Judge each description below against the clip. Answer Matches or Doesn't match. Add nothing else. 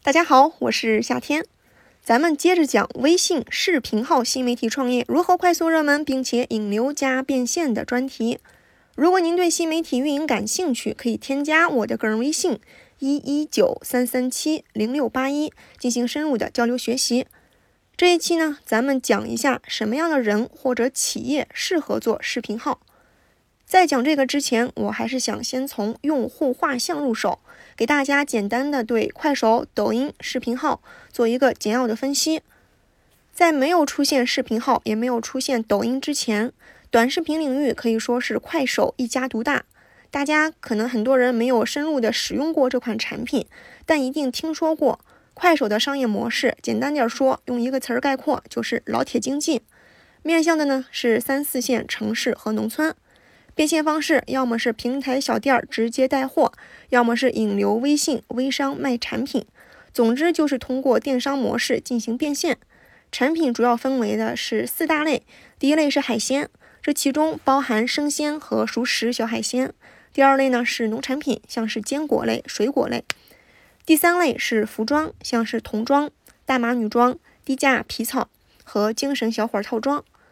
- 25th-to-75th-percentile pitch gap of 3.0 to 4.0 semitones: Matches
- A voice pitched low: Doesn't match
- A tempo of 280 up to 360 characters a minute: Doesn't match